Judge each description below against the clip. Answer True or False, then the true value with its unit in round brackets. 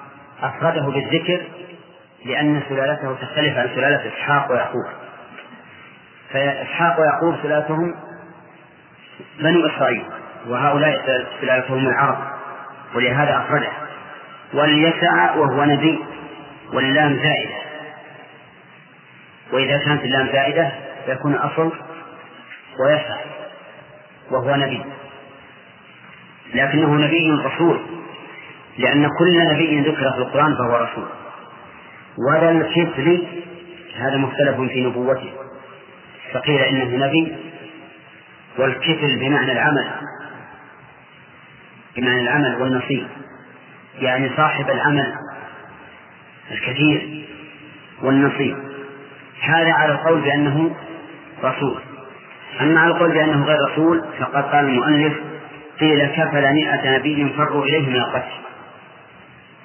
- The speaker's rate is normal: False (85 wpm)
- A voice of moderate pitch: True (145 Hz)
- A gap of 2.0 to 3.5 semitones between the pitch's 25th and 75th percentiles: True (2.5 semitones)